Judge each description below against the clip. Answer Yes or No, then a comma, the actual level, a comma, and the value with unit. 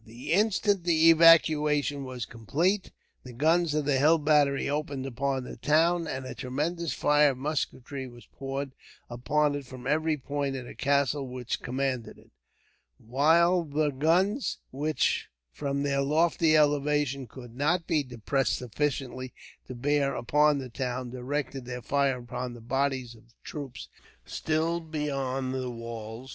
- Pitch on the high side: No, medium, 140 Hz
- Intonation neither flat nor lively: Yes, average, 3.0 semitones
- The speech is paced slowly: No, average, 150 wpm